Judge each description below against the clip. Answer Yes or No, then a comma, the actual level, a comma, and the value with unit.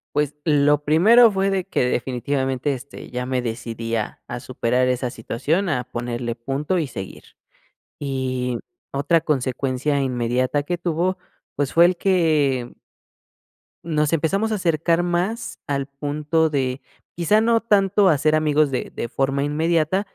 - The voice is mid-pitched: Yes, medium, 145 Hz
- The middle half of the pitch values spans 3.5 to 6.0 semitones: Yes, average, 4.9 semitones